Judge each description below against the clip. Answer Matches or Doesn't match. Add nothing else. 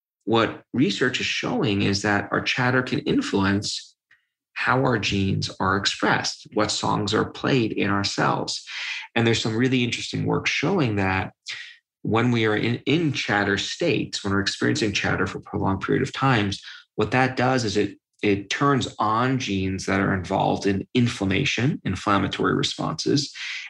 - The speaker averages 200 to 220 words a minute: Doesn't match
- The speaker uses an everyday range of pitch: Matches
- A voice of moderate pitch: Doesn't match